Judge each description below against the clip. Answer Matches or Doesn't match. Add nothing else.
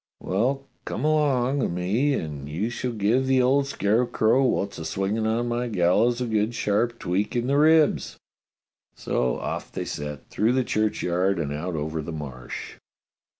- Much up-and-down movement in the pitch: Matches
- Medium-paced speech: Matches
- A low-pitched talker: Matches